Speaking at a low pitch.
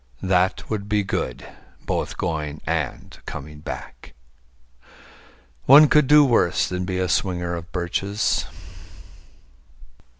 Yes: very low, 90 Hz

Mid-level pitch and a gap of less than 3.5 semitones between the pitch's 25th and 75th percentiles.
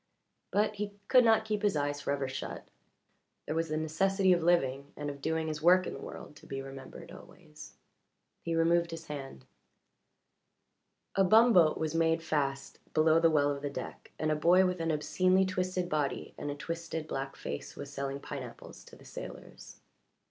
No: medium, 160 Hz; average, 4.1 semitones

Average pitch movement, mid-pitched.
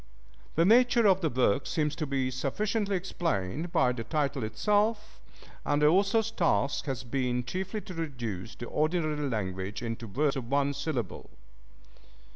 No: wide, 6.5 semitones; medium, 145 Hz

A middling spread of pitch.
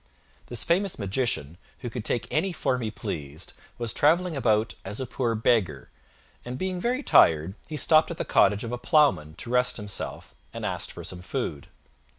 No: wide, 7.2 semitones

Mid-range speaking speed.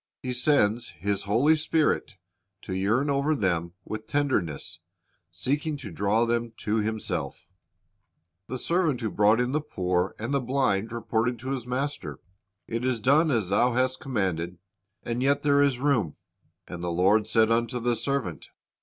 Yes: average, 160 wpm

